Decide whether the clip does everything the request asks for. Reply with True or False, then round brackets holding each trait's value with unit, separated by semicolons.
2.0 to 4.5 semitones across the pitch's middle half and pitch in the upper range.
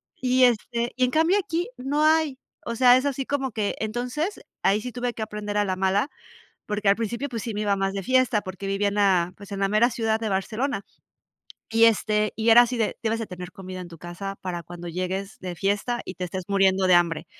True (4.2 semitones; 210 Hz)